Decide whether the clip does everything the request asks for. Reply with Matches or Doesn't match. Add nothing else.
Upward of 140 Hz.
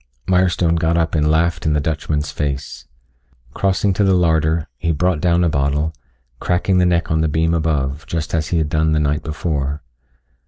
Doesn't match